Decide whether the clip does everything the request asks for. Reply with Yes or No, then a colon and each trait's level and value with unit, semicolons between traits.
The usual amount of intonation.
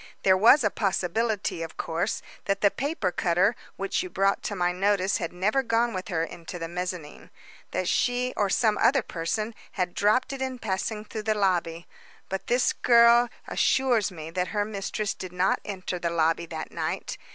Yes: average, 4.2 semitones